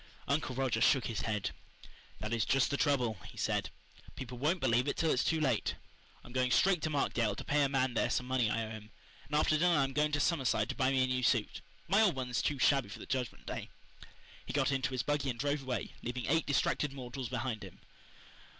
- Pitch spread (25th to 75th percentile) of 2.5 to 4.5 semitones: Yes, average, 3.0 semitones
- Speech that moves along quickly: Yes, fast, 230 wpm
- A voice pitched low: Yes, low, 130 Hz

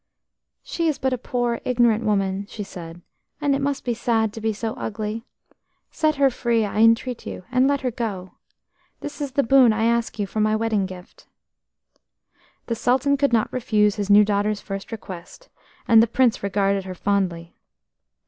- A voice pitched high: Yes, high, 225 Hz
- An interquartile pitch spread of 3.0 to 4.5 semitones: Yes, average, 3.8 semitones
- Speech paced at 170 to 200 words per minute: Yes, average, 180 wpm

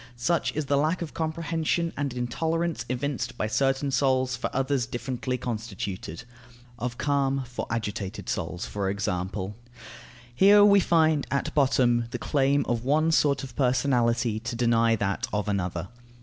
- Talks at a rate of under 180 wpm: Yes, average, 150 wpm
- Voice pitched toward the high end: No, low, 125 Hz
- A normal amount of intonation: Yes, average, 3.8 semitones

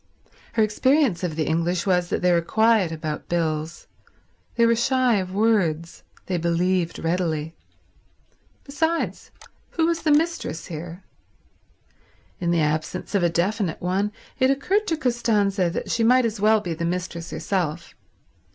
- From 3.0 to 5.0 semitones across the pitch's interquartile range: No, wide, 5.5 semitones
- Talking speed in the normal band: Yes, average, 150 wpm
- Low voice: No, medium, 185 Hz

